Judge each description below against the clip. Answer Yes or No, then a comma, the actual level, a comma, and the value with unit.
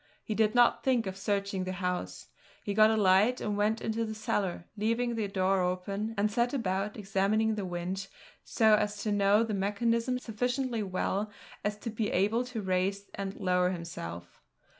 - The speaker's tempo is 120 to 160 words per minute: No, average, 180 wpm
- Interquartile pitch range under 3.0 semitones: Yes, narrow, 2.6 semitones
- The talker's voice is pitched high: Yes, high, 205 Hz